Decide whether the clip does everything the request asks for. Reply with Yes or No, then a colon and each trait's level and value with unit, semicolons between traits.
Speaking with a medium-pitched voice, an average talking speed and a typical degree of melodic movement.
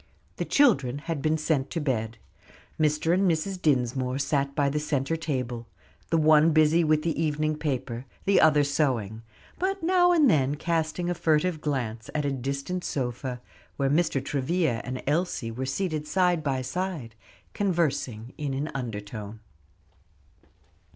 Yes: medium, 150 Hz; average, 150 wpm; average, 4.0 semitones